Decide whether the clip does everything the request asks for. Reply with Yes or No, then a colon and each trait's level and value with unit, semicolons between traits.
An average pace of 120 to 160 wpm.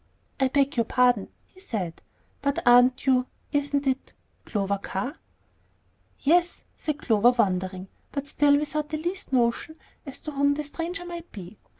Yes: average, 155 wpm